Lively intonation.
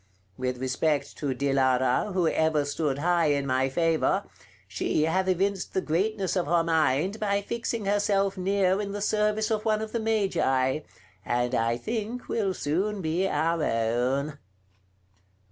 Yes: wide, 6.4 semitones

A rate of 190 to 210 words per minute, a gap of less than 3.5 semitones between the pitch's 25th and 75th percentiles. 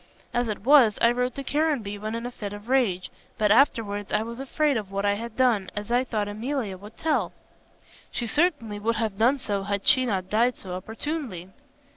No: fast, 205 wpm; average, 3.8 semitones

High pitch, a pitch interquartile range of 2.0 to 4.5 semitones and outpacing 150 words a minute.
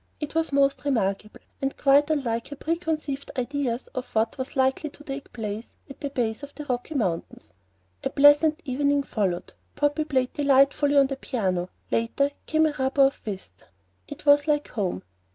Yes: very high, 275 Hz; average, 3.9 semitones; average, 170 wpm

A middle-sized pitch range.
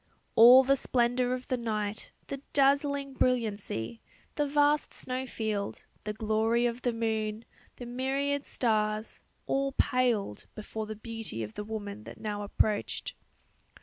Yes: average, 3.4 semitones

